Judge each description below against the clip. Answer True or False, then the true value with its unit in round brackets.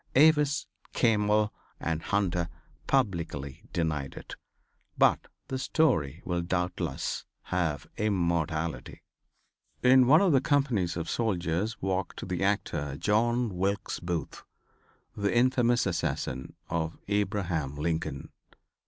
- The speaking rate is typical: False (105 wpm)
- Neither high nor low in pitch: False (95 Hz)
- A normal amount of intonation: False (5.9 semitones)